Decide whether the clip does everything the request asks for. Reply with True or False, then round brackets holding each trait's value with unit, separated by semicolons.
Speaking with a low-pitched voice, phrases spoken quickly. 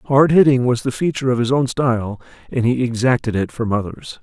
True (125 Hz; 215 wpm)